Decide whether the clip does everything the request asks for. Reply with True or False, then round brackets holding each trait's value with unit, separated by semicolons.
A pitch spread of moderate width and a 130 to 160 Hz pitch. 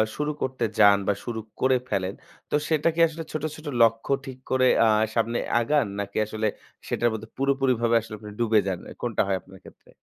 False (3.7 semitones; 115 Hz)